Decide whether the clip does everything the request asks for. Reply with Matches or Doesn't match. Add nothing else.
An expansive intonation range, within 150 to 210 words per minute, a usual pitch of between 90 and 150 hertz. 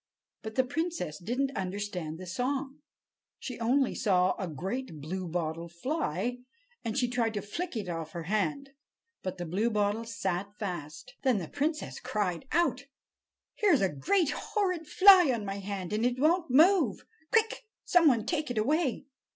Doesn't match